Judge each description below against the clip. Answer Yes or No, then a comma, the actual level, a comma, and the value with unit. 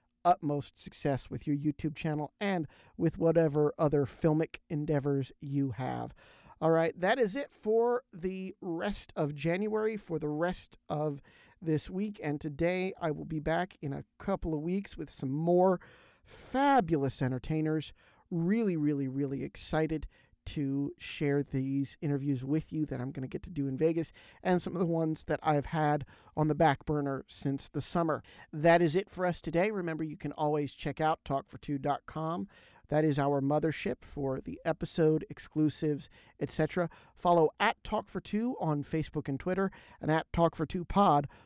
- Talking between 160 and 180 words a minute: Yes, average, 170 wpm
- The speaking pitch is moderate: Yes, medium, 155 Hz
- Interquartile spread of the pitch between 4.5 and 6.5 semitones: No, average, 3.3 semitones